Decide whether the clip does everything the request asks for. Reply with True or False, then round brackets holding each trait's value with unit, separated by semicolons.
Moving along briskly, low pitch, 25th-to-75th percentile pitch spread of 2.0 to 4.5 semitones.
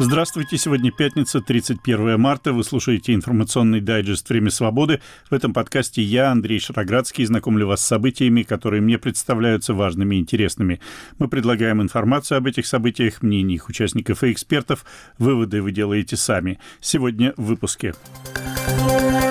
False (135 wpm; 115 Hz; 3.4 semitones)